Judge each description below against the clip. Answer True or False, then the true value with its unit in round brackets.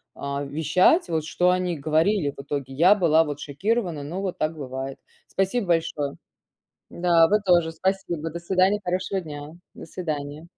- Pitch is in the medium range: True (165 Hz)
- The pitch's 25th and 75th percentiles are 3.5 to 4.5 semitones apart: True (4.0 semitones)